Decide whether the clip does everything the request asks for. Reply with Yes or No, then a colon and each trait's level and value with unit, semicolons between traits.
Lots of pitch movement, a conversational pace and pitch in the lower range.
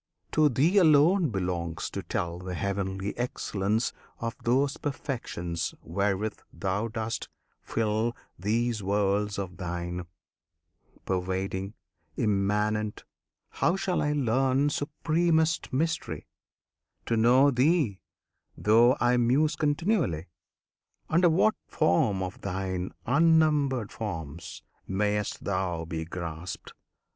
No: wide, 6.9 semitones; slow, 100 wpm; low, 110 Hz